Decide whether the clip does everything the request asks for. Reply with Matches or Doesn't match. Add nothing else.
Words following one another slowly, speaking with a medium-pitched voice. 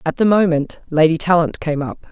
Doesn't match